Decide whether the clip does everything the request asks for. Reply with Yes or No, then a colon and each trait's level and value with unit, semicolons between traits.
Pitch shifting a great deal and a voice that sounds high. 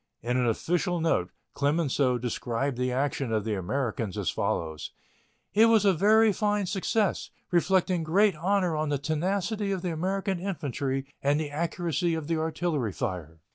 No: wide, 6.4 semitones; medium, 160 Hz